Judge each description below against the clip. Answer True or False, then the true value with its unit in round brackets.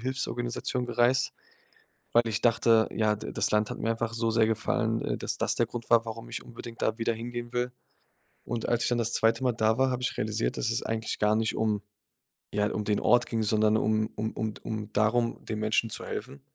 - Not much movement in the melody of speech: True (1.6 semitones)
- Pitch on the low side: True (115 Hz)